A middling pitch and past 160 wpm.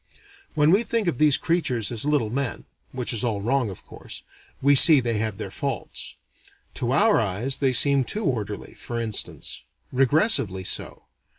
No: low, 130 Hz; average, 170 wpm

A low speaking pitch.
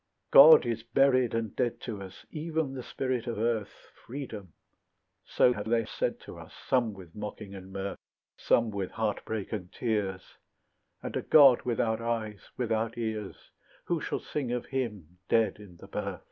Yes: low, 115 Hz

